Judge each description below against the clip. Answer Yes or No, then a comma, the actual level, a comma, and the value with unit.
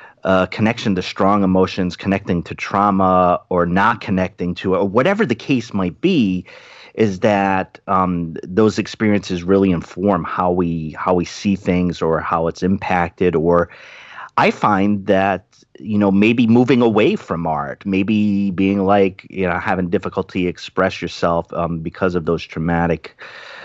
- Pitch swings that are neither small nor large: No, narrow, 2.2 semitones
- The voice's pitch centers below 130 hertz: Yes, very low, 95 Hz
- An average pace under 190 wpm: Yes, average, 150 wpm